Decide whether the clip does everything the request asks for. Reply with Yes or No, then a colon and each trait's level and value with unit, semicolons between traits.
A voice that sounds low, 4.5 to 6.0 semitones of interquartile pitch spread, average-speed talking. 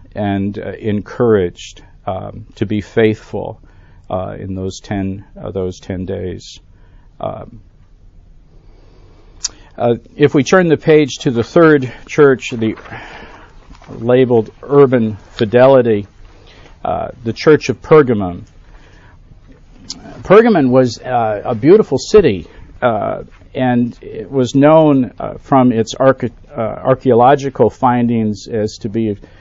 No: low, 110 Hz; average, 5.2 semitones; slow, 115 wpm